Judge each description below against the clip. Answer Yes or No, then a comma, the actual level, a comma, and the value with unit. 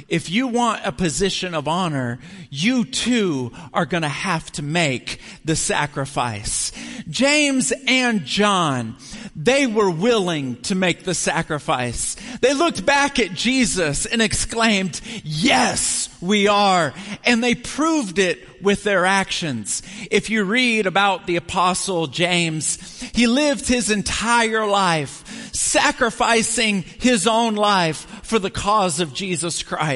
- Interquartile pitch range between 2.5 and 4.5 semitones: No, average, 5.3 semitones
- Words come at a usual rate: No, slow, 130 wpm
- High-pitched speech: Yes, high, 195 Hz